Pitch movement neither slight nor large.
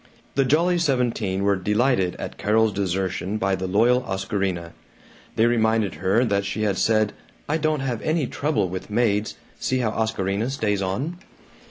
Yes: average, 4.4 semitones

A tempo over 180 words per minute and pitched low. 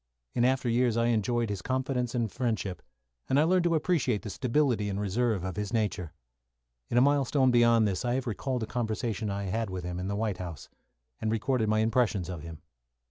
Yes: fast, 205 wpm; low, 115 Hz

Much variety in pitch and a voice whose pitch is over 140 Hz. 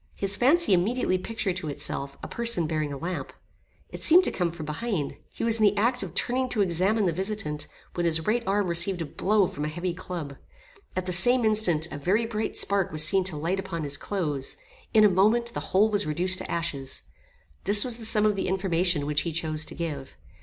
No: average, 4.9 semitones; medium, 185 Hz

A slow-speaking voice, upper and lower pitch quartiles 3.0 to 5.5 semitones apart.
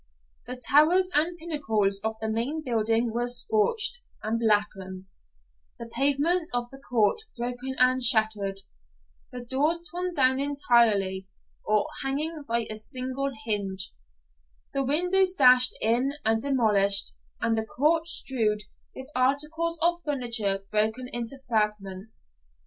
Yes: slow, 125 wpm; average, 4.6 semitones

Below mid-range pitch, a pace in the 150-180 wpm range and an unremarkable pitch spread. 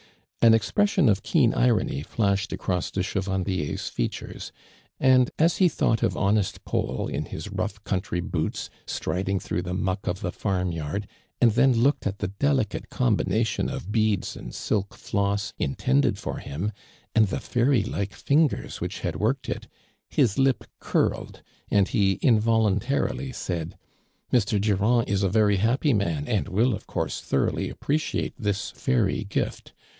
Yes: low, 105 Hz; average, 155 wpm; average, 3.7 semitones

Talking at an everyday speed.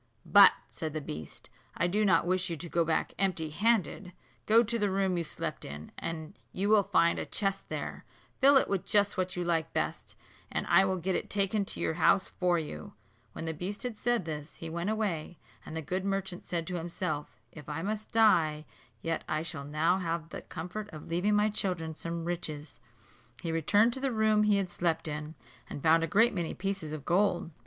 No: fast, 215 wpm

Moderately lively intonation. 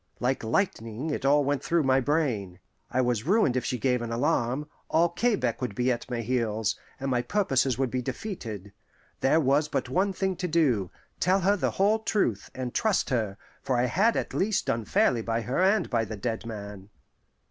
No: wide, 6.5 semitones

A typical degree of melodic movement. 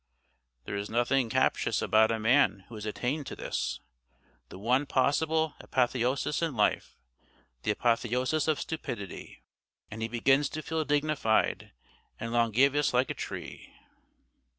Yes: average, 4.4 semitones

